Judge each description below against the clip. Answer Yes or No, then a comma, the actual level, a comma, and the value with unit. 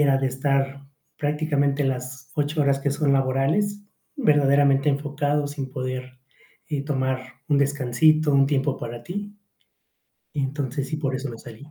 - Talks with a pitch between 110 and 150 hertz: Yes, medium, 140 Hz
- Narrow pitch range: Yes, narrow, 1.8 semitones